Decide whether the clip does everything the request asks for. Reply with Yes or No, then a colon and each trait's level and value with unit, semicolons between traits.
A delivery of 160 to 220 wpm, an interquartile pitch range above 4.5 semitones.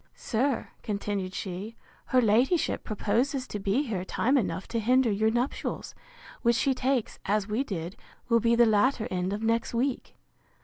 No: average, 165 wpm; average, 3.7 semitones